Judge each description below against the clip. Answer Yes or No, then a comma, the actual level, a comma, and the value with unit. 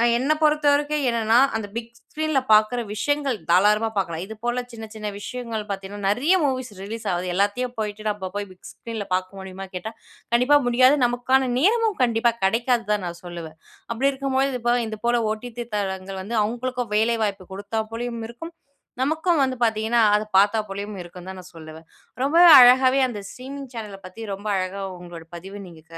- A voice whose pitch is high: Yes, high, 225 Hz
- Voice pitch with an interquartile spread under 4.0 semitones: No, average, 4.4 semitones